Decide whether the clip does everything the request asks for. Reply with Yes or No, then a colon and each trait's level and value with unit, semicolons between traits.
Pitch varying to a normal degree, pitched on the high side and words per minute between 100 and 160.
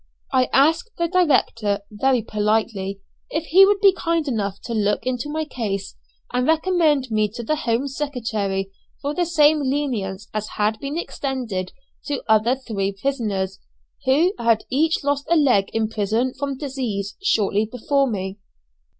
No: wide, 5.7 semitones; very high, 250 Hz; average, 155 wpm